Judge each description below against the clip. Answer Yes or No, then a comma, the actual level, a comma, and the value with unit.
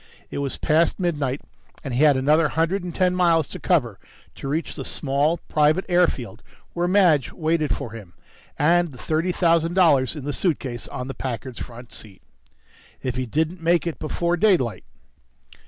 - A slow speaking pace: No, average, 170 wpm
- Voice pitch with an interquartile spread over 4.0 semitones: Yes, average, 4.7 semitones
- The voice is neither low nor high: Yes, medium, 155 Hz